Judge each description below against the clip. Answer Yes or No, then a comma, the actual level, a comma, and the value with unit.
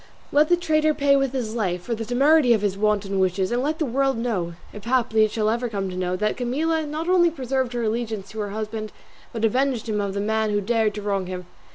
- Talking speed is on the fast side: Yes, fast, 245 wpm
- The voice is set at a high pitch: Yes, high, 225 Hz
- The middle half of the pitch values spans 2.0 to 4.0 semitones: No, average, 4.6 semitones